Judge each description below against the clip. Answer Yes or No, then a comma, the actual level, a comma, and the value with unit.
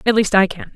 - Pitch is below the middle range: No, high, 200 Hz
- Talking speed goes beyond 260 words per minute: Yes, fast, 320 wpm